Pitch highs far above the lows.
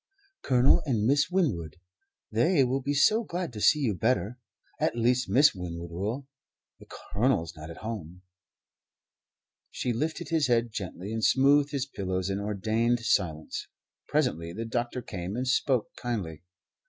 Yes: wide, 6.1 semitones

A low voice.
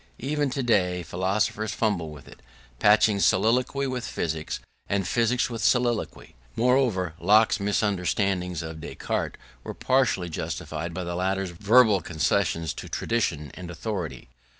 Yes: low, 100 Hz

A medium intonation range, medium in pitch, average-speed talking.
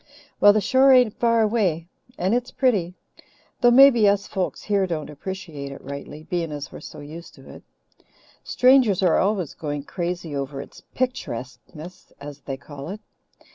No: wide, 6.7 semitones; medium, 180 Hz; average, 165 wpm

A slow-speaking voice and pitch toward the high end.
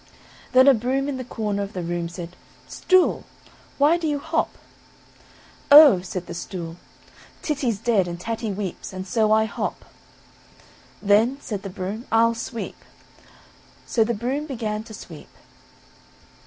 No: average, 145 wpm; high, 220 Hz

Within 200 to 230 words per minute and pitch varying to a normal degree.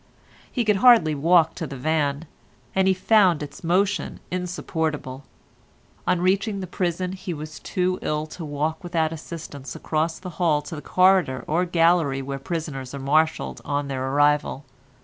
No: average, 160 wpm; average, 3.8 semitones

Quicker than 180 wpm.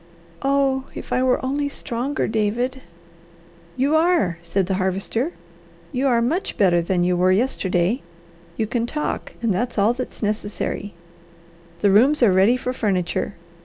No: average, 150 wpm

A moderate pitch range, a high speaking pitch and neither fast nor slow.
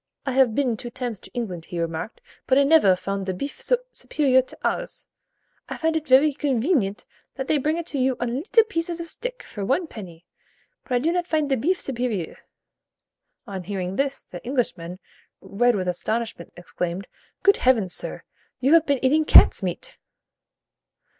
No: wide, 7.3 semitones; very high, 255 Hz; average, 180 wpm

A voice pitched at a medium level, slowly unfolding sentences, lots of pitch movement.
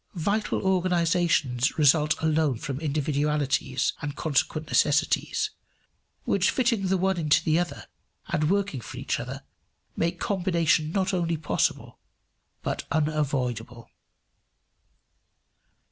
No: medium, 155 Hz; slow, 105 wpm; average, 3.8 semitones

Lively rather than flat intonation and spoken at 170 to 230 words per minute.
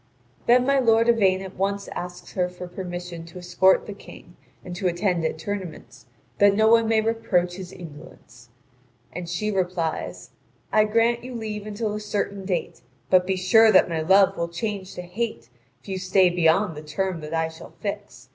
No: average, 3.2 semitones; average, 185 wpm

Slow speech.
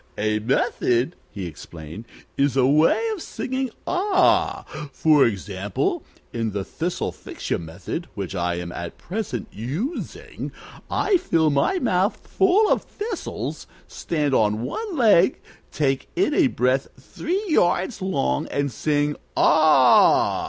Yes: slow, 125 wpm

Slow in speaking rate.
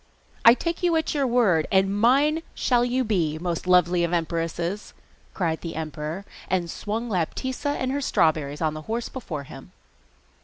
No: average, 165 wpm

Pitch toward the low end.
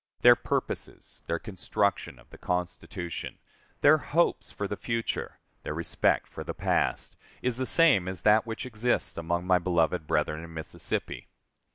Yes: very low, 95 Hz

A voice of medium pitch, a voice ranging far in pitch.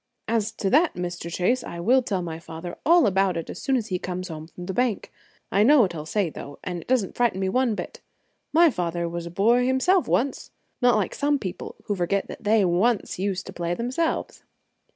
No: high, 195 Hz; wide, 5.8 semitones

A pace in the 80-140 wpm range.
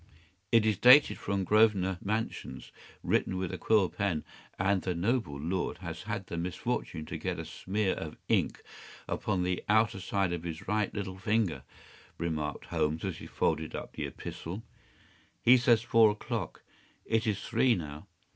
No: average, 165 wpm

